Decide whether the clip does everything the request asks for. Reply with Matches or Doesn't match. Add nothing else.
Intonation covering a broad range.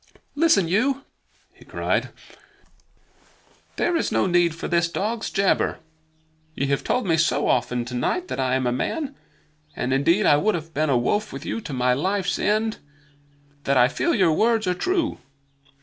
Matches